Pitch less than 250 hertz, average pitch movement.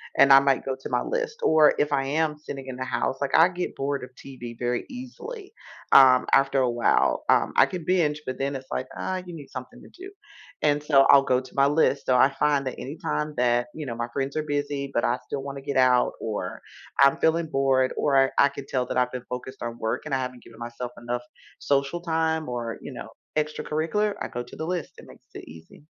Yes: medium, 140 Hz; average, 3.2 semitones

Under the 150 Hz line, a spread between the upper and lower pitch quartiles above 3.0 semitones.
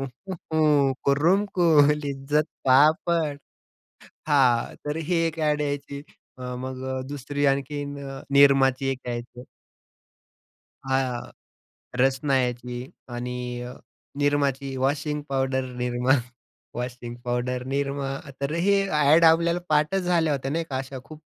No: medium, 140 Hz; narrow, 2.5 semitones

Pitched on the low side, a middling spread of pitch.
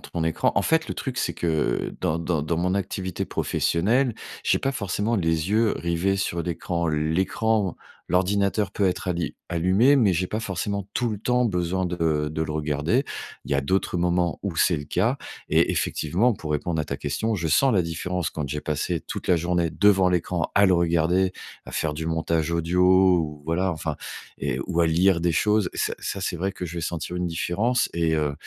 Yes: very low, 90 Hz; average, 3.2 semitones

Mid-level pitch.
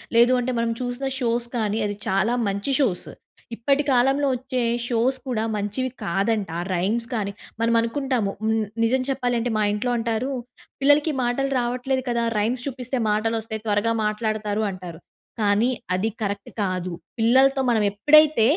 No: high, 230 Hz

